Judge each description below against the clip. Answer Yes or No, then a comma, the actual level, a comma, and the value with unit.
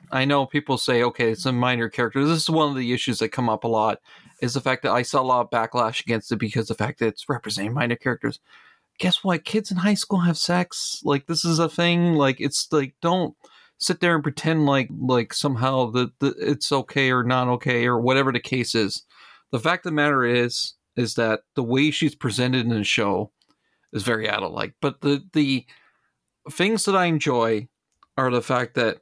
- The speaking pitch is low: Yes, low, 130 Hz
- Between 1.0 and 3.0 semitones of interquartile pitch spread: No, average, 4.2 semitones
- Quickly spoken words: Yes, fast, 220 wpm